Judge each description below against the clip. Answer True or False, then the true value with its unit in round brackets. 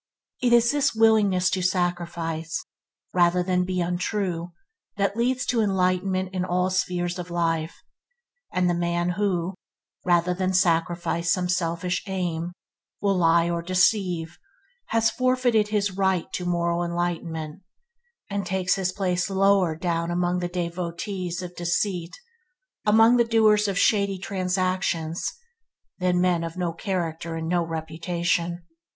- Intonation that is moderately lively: False (1.9 semitones)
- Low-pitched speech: False (180 Hz)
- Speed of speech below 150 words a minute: True (135 wpm)